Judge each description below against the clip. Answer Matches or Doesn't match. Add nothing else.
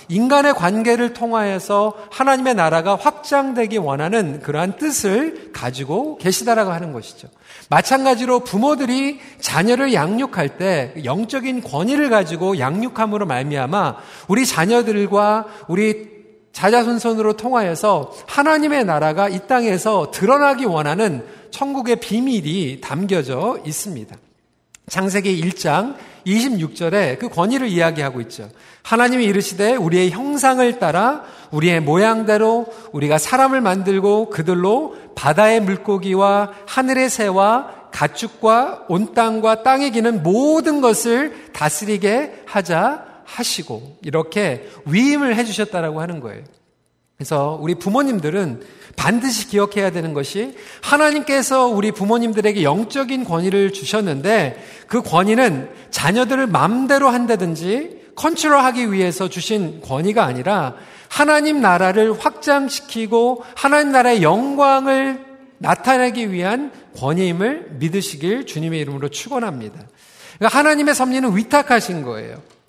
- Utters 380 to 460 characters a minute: Doesn't match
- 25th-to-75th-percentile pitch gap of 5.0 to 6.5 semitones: Matches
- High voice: Matches